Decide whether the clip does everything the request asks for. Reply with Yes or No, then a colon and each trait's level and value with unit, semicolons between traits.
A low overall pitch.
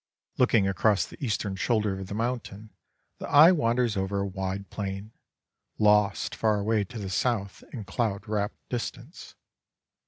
Yes: low, 105 Hz